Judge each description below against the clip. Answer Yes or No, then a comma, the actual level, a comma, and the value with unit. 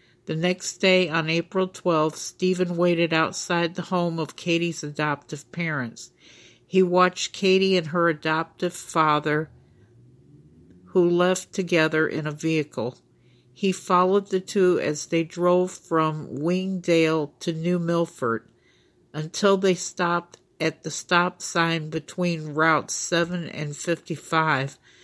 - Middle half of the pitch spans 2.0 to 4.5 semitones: Yes, narrow, 2.6 semitones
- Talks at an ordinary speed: No, slow, 125 wpm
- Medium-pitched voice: Yes, medium, 170 Hz